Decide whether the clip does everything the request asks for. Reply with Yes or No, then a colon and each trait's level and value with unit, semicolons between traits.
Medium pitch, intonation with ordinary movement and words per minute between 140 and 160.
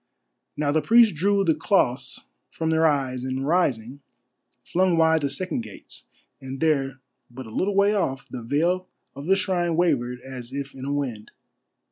No: medium, 145 Hz; average, 4.9 semitones; average, 170 wpm